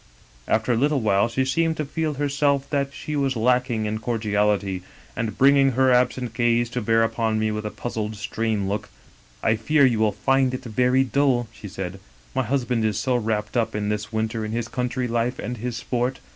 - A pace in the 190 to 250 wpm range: Yes, fast, 205 wpm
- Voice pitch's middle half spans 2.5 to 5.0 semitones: Yes, average, 3.3 semitones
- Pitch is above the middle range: No, low, 120 Hz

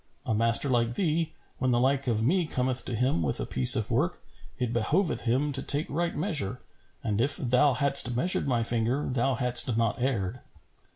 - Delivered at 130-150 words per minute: No, average, 190 wpm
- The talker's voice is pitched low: Yes, low, 125 Hz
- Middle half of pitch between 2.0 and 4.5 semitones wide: Yes, average, 3.5 semitones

